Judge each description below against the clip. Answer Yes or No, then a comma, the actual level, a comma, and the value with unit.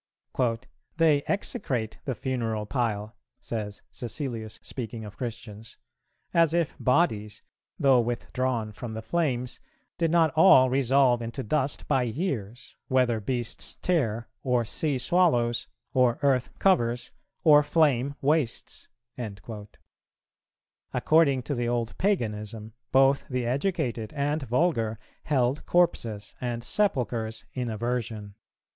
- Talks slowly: Yes, slow, 115 wpm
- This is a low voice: Yes, low, 125 Hz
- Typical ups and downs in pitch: Yes, average, 4.0 semitones